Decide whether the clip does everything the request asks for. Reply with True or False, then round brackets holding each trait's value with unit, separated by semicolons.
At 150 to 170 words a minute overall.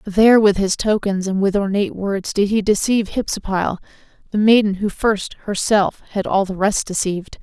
False (180 wpm)